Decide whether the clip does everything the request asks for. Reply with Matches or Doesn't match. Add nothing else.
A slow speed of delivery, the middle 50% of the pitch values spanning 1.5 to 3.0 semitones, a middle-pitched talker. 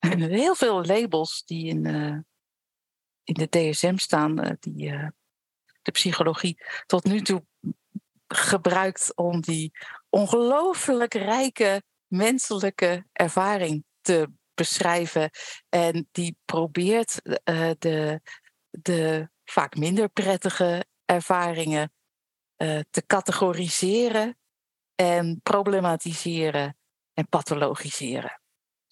Doesn't match